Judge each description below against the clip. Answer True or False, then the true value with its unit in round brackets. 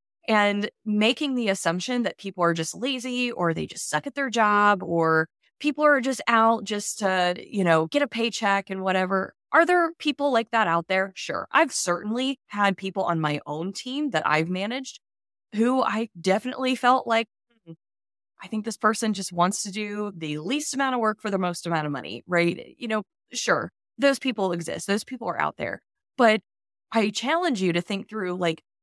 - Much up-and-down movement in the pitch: True (5.8 semitones)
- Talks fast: False (195 wpm)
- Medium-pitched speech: False (210 Hz)